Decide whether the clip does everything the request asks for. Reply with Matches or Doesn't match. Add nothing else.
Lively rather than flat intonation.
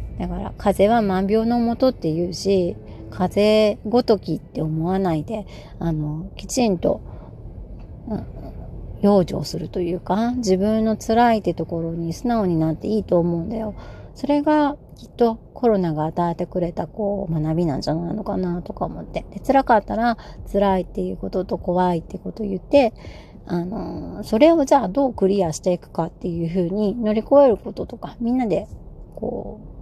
Doesn't match